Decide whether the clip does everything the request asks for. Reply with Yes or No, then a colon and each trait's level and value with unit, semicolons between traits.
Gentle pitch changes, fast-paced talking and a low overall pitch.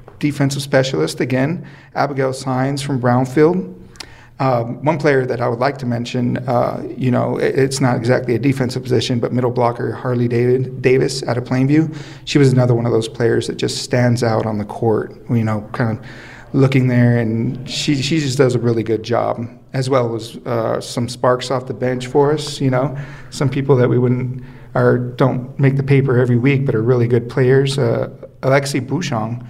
No: narrow, 2.1 semitones; average, 195 wpm; low, 125 Hz